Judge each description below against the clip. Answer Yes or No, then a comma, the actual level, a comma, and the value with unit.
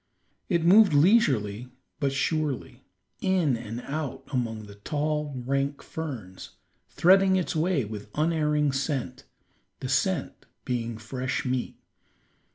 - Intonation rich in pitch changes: No, average, 4.6 semitones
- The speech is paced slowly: Yes, slow, 115 wpm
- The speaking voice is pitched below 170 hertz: Yes, medium, 140 Hz